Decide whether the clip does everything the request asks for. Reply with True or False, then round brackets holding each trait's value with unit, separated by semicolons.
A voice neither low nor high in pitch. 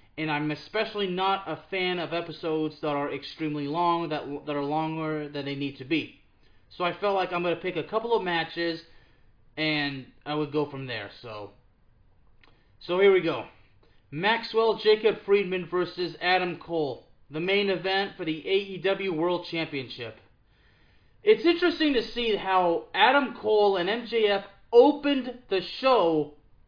True (170 Hz)